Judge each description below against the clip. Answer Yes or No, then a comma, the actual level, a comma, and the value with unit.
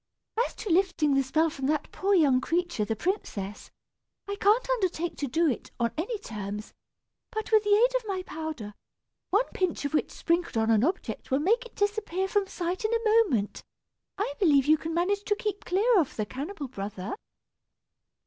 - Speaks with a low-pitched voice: No, very high, 345 Hz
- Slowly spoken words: No, average, 185 wpm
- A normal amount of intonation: No, wide, 7.1 semitones